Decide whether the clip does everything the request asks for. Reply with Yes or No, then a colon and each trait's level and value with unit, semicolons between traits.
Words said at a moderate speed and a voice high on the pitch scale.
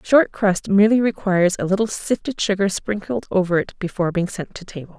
Yes: average, 195 wpm; high, 195 Hz